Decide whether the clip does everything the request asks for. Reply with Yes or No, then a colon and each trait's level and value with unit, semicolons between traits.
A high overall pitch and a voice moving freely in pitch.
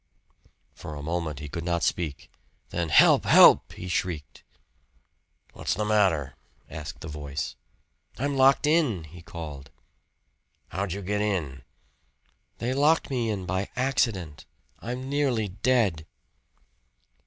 No: very low, 90 Hz; wide, 7.3 semitones